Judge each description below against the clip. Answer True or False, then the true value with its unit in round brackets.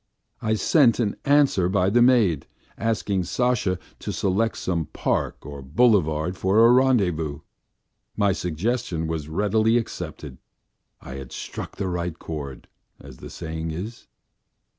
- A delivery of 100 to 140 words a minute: True (135 wpm)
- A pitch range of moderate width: False (6.0 semitones)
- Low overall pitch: True (95 Hz)